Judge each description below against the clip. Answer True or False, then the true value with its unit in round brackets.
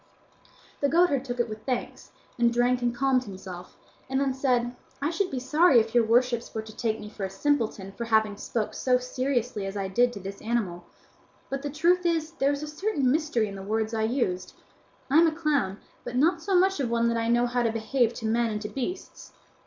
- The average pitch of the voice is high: True (245 Hz)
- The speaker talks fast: True (230 wpm)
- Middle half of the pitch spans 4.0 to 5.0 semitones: True (4.3 semitones)